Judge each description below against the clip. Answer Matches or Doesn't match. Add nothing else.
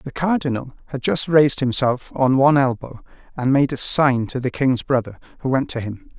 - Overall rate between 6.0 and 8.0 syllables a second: Doesn't match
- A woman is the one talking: Doesn't match